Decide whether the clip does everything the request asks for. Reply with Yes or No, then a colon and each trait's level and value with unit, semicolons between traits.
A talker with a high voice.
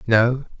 No: low, 120 Hz